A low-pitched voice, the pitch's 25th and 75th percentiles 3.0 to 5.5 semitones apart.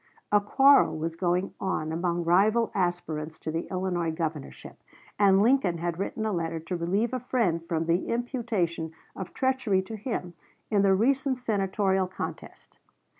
No: high, 190 Hz; average, 4.5 semitones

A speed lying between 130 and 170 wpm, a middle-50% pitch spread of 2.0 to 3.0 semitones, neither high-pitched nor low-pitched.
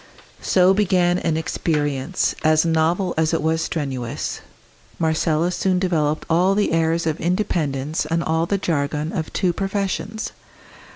Yes: slow, 135 wpm; narrow, 2.6 semitones; medium, 165 Hz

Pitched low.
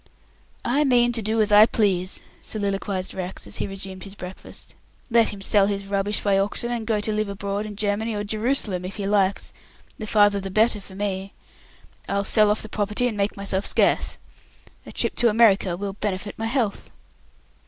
No: high, 205 Hz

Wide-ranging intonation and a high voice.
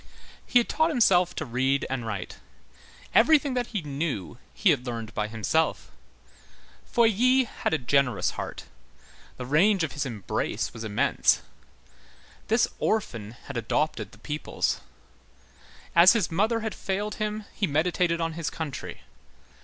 No: wide, 9.0 semitones; medium, 165 Hz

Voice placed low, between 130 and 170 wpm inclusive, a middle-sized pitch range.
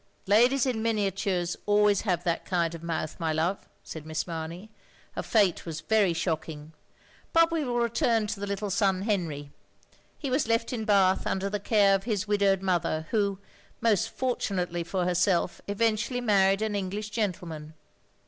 No: high, 195 Hz; average, 165 wpm; average, 3.9 semitones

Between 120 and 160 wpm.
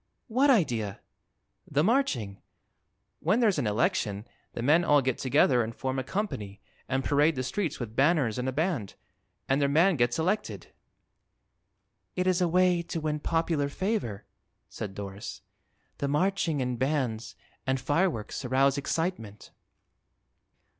Yes: average, 140 wpm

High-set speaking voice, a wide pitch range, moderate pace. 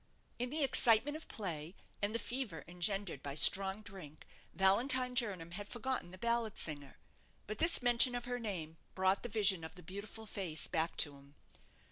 Yes: high, 200 Hz; wide, 5.7 semitones; average, 175 wpm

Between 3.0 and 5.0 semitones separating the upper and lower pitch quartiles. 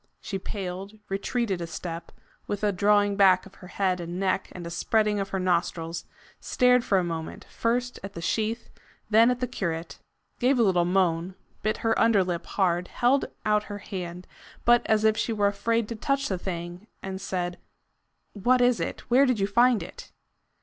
Yes: average, 4.0 semitones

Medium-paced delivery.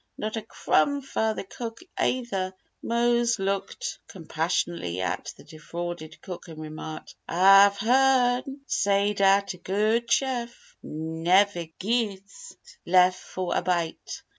No: slow, 120 wpm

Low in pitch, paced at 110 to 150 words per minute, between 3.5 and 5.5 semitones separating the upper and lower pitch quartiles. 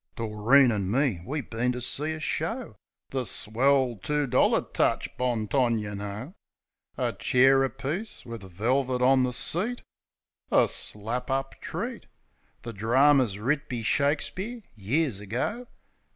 Yes: low, 125 Hz; average, 140 wpm; average, 4.0 semitones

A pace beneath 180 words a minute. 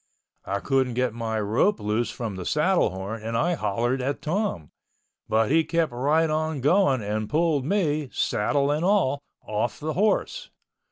Yes: average, 150 wpm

